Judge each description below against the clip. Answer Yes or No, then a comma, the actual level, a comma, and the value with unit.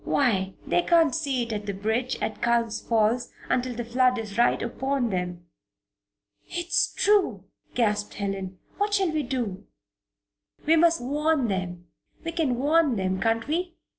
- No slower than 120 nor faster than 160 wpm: Yes, average, 155 wpm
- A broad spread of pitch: Yes, wide, 6.5 semitones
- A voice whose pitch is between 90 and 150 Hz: No, high, 240 Hz